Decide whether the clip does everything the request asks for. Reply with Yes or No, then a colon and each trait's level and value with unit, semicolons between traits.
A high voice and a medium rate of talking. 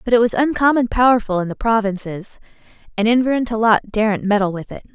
Yes: high, 220 Hz; average, 195 wpm